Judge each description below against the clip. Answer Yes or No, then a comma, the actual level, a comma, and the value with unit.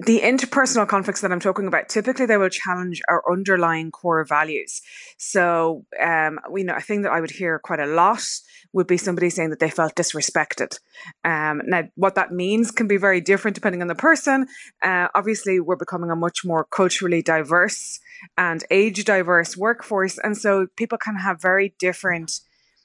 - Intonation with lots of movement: No, average, 3.6 semitones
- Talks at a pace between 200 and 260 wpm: No, average, 180 wpm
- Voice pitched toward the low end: No, medium, 185 Hz